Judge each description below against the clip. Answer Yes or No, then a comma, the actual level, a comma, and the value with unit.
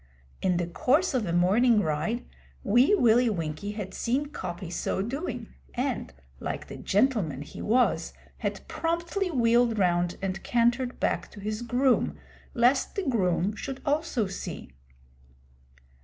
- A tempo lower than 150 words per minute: Yes, average, 140 wpm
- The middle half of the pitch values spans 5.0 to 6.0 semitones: Yes, wide, 5.5 semitones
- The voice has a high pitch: Yes, high, 230 Hz